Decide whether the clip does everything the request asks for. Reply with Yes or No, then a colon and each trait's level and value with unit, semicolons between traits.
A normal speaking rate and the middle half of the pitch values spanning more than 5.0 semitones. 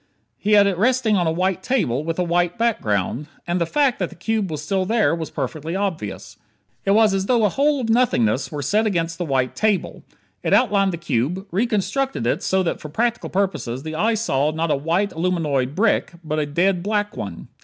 No: fast, 210 wpm; wide, 5.4 semitones